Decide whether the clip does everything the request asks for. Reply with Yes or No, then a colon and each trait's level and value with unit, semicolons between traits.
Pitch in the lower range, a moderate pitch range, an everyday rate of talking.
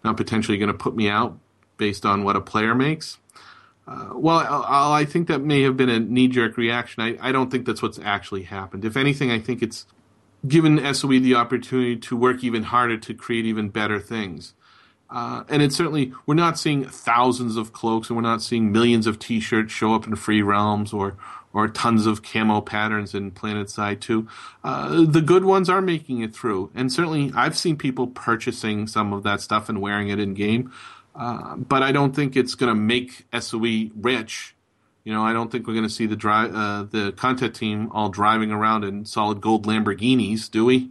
No: low, 115 Hz; average, 3.1 semitones; fast, 215 wpm